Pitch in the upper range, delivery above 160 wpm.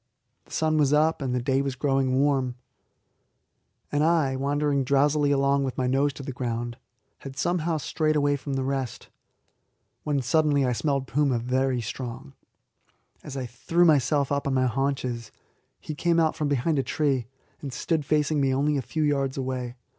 No: medium, 140 Hz; average, 175 wpm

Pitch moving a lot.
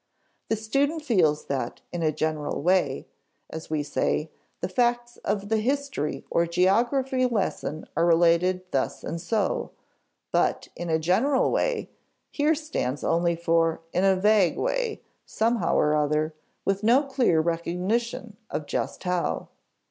Yes: wide, 6.5 semitones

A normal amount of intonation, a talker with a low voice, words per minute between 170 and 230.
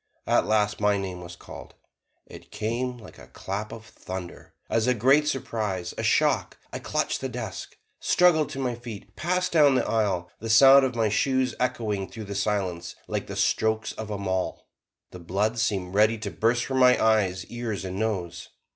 Yes: average, 4.0 semitones; low, 110 Hz; average, 185 wpm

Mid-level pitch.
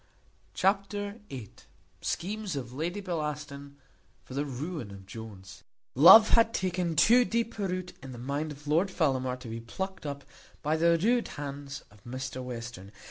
Yes: medium, 150 Hz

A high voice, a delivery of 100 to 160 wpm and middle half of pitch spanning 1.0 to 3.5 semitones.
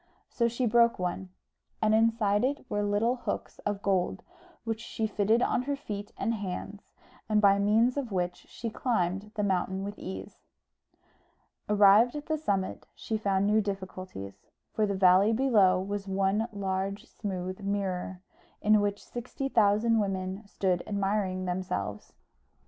Yes: high, 205 Hz; average, 150 wpm; average, 2.7 semitones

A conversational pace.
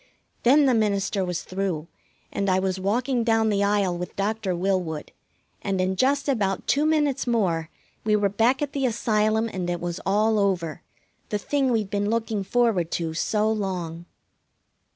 Yes: average, 170 wpm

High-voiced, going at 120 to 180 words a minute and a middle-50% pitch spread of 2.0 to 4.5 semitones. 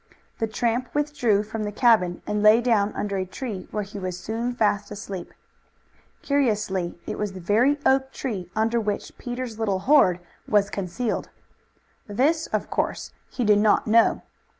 Yes: high, 215 Hz; average, 160 wpm; average, 3.3 semitones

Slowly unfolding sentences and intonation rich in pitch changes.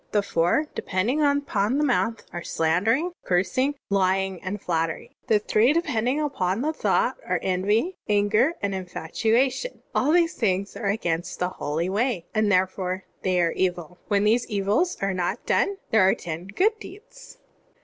No: average, 160 wpm; wide, 5.8 semitones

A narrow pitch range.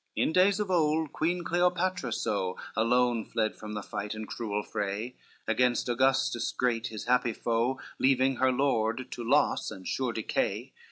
No: average, 3.6 semitones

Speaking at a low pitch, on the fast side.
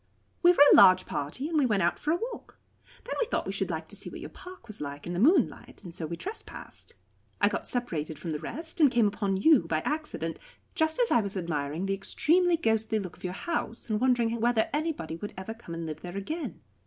No: high, 220 Hz; fast, 240 wpm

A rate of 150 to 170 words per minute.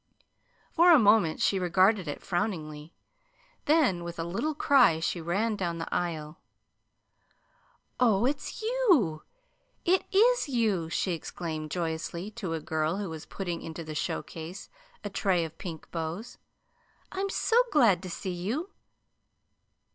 No: average, 140 wpm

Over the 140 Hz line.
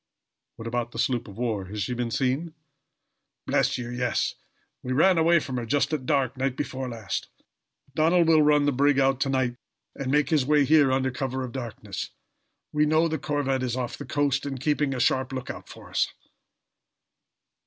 No: low, 135 Hz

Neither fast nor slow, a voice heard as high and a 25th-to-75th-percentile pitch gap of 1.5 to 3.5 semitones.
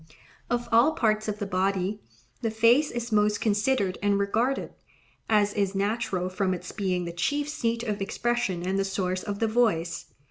Yes: average, 175 wpm; high, 210 Hz; average, 3.2 semitones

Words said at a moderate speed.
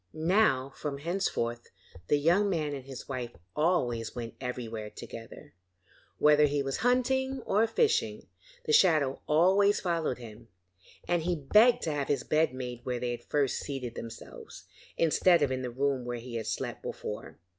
Yes: average, 165 wpm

